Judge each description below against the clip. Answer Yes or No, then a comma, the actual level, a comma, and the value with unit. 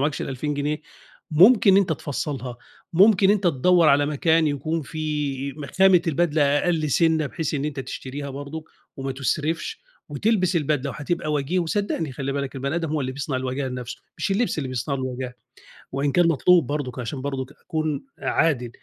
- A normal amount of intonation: Yes, average, 3.3 semitones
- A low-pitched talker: No, medium, 150 Hz